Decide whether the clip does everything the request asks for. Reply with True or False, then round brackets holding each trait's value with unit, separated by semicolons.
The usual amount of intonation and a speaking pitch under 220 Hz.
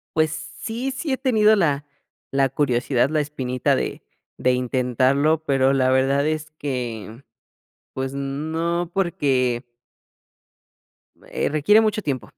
True (3.6 semitones; 140 Hz)